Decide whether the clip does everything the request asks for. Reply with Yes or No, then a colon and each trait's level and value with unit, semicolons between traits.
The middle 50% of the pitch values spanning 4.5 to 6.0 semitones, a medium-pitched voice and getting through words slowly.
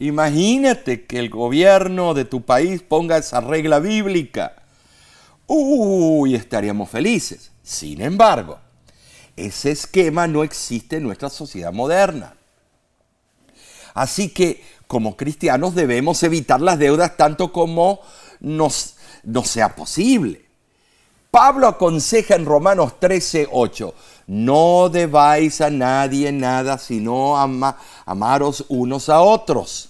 Yes: wide, 5.5 semitones; medium, 150 Hz; slow, 110 wpm